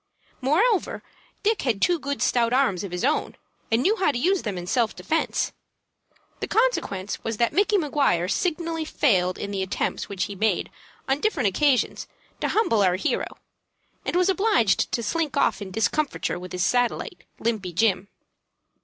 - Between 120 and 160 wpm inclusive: No, average, 170 wpm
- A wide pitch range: Yes, wide, 8.6 semitones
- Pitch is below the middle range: No, high, 245 Hz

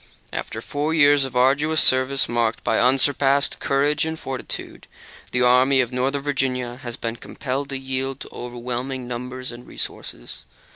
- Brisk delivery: No, average, 150 wpm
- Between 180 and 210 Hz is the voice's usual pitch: No, low, 130 Hz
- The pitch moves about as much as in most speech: No, narrow, 1.9 semitones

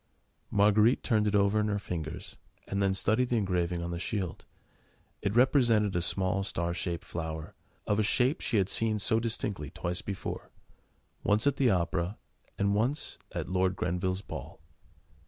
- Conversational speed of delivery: Yes, average, 165 wpm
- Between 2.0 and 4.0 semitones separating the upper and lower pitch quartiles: Yes, average, 3.3 semitones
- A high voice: No, low, 100 Hz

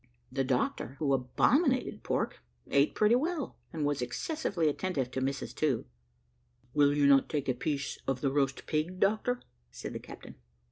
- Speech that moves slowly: No, average, 160 wpm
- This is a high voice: No, medium, 145 Hz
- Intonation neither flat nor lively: No, wide, 5.9 semitones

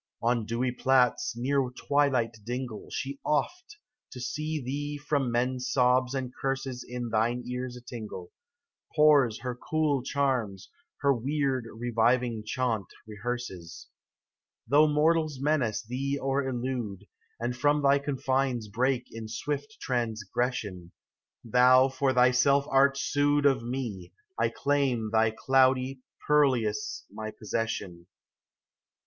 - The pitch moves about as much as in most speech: Yes, average, 3.0 semitones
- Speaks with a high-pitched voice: No, low, 125 Hz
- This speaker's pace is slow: Yes, slow, 120 wpm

